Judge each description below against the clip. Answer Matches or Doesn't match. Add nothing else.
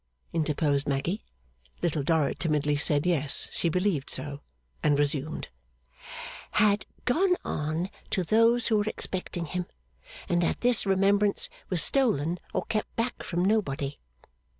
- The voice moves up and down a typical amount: Doesn't match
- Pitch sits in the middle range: Matches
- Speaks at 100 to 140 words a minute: Matches